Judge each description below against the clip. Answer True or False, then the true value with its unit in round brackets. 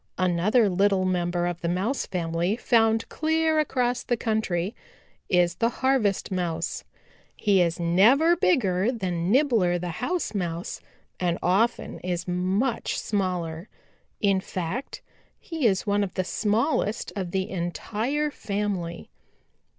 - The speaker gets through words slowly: True (125 wpm)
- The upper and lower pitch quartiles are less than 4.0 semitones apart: False (4.8 semitones)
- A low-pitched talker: False (195 Hz)